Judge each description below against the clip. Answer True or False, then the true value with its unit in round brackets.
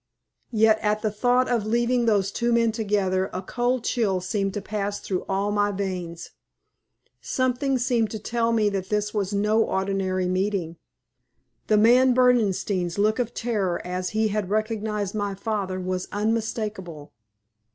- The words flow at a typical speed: True (150 wpm)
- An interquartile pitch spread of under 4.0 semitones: True (2.9 semitones)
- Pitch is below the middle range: False (210 Hz)